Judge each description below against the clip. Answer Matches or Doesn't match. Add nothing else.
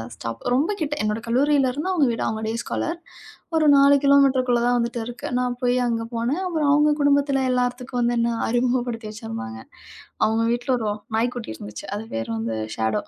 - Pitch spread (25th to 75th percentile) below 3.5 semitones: Doesn't match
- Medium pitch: Doesn't match